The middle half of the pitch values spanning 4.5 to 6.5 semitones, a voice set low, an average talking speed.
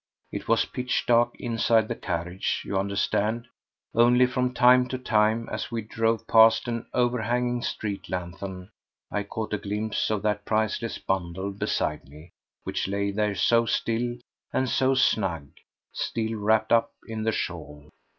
No: average, 3.0 semitones; low, 110 Hz; average, 150 wpm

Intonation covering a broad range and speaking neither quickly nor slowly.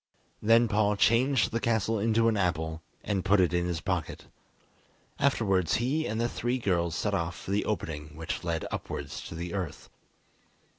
No: average, 4.9 semitones; average, 170 wpm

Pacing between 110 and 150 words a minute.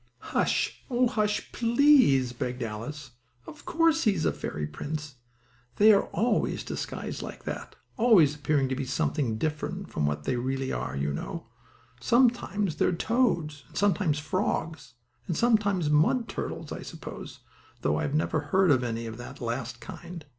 No: average, 160 wpm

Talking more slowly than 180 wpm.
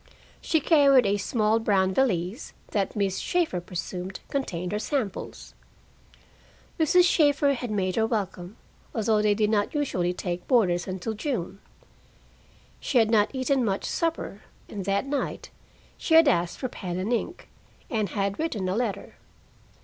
Yes: average, 150 wpm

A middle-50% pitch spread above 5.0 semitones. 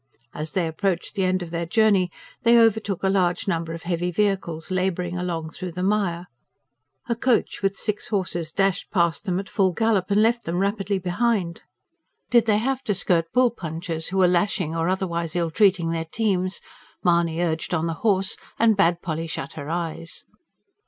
No: average, 3.2 semitones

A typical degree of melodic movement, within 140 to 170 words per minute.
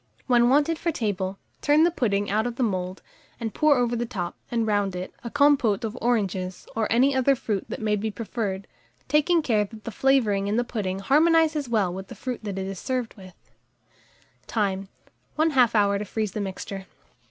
No: average, 4.5 semitones; average, 195 wpm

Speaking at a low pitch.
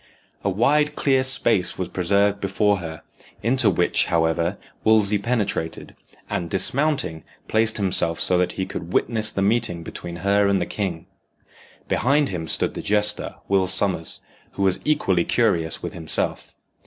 Yes: low, 100 Hz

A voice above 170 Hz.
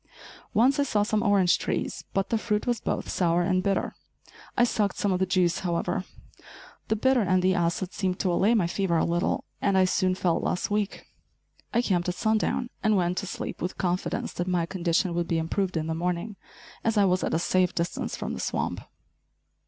Yes: medium, 185 Hz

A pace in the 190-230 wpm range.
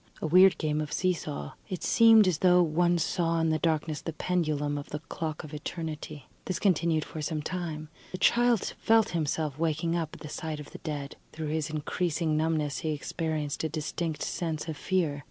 Yes: average, 195 wpm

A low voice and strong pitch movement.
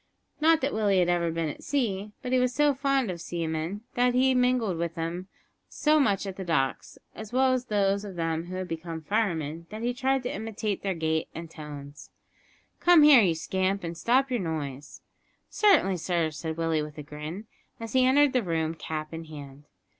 No: medium, 185 Hz; wide, 7.3 semitones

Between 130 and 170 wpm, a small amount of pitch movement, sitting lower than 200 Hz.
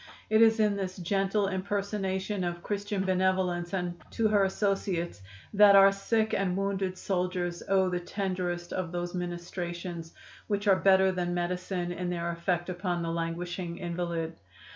Yes: average, 150 wpm; narrow, 2.0 semitones; medium, 185 Hz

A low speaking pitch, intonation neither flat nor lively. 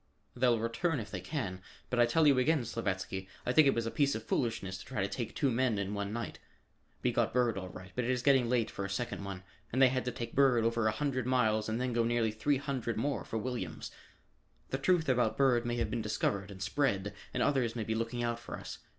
Yes: low, 120 Hz; average, 3.0 semitones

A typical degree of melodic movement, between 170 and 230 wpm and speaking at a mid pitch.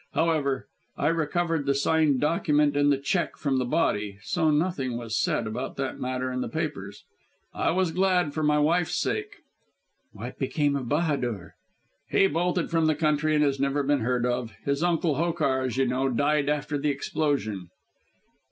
Yes: average, 3.5 semitones; average, 175 wpm; medium, 145 Hz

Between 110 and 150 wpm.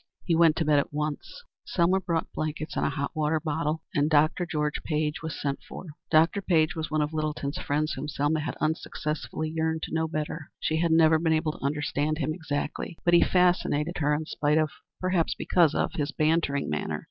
No: fast, 205 wpm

